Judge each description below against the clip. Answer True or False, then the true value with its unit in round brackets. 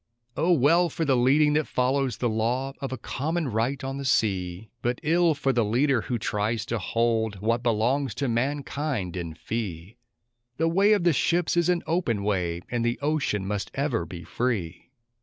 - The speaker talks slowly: False (185 wpm)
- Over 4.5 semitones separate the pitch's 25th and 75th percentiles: True (5.2 semitones)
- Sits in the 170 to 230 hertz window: False (125 Hz)